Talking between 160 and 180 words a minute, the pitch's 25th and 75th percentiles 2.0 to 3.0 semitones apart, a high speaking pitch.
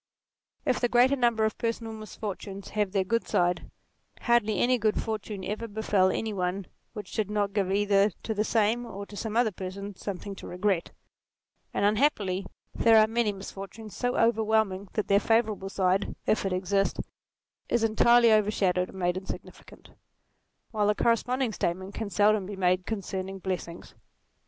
Yes: average, 165 wpm; narrow, 2.5 semitones; high, 205 Hz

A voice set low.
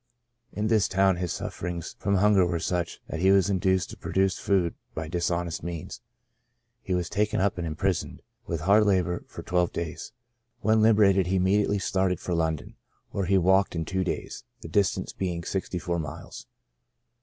Yes: very low, 95 Hz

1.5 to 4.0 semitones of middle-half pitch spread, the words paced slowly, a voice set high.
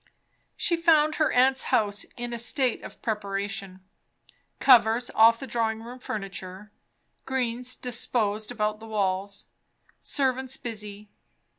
Yes: average, 3.4 semitones; slow, 120 wpm; high, 225 Hz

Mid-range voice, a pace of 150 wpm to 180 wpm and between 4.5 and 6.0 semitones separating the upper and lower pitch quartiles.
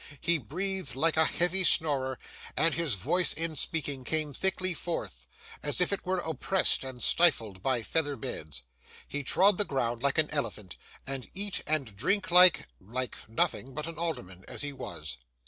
Yes: medium, 150 Hz; average, 165 wpm; average, 5.2 semitones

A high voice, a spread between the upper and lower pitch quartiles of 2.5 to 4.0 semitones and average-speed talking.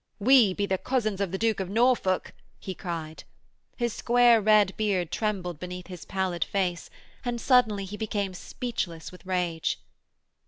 Yes: high, 195 Hz; average, 3.6 semitones; average, 155 wpm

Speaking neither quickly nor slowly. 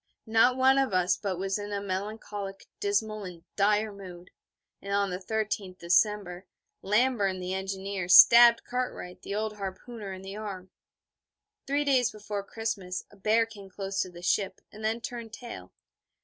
Yes: average, 165 wpm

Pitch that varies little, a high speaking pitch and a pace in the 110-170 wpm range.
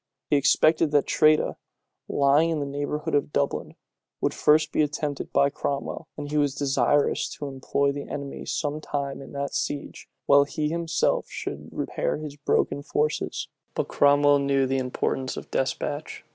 No: narrow, 1.3 semitones; medium, 145 Hz; average, 160 wpm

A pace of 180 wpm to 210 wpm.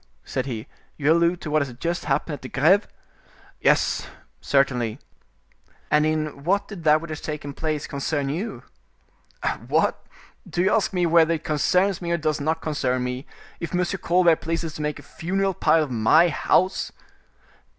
No: average, 170 wpm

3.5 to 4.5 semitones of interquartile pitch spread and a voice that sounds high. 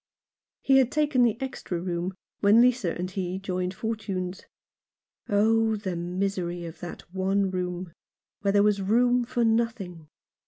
Yes: average, 3.9 semitones; high, 195 Hz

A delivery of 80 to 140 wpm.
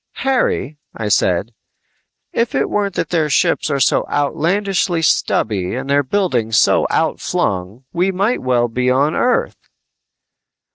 Yes: slow, 135 wpm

